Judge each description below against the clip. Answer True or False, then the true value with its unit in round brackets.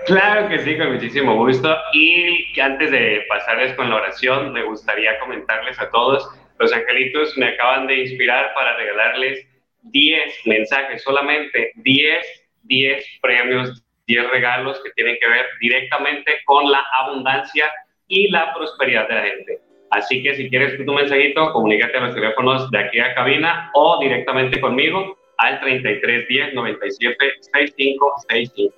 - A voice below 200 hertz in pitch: True (135 Hz)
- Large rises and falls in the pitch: False (3.1 semitones)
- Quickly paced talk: False (150 wpm)